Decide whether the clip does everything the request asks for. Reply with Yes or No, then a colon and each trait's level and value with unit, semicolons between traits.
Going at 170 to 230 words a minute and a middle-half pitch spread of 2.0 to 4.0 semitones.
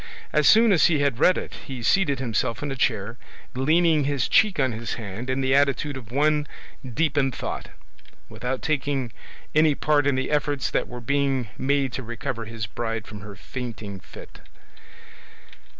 Yes: average, 175 wpm; average, 3.7 semitones